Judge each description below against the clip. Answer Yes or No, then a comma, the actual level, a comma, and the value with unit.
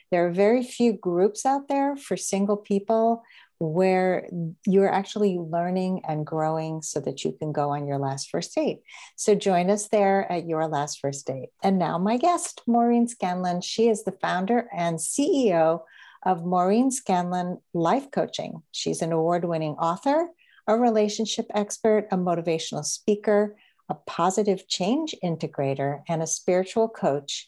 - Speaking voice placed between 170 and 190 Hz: Yes, medium, 185 Hz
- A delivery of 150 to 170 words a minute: Yes, average, 155 wpm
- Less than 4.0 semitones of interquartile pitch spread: No, average, 4.7 semitones